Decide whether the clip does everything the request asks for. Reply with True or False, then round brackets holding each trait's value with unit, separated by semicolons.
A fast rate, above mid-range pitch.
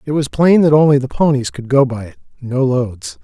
False (225 wpm; 135 Hz)